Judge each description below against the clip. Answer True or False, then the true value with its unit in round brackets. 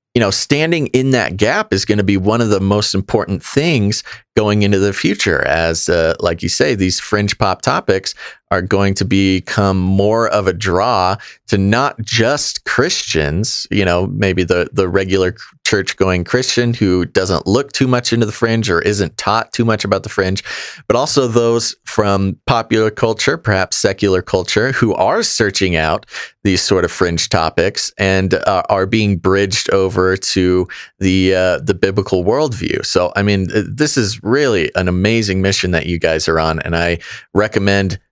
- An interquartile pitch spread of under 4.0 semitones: True (3.0 semitones)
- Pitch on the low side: True (100 Hz)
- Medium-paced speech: True (180 wpm)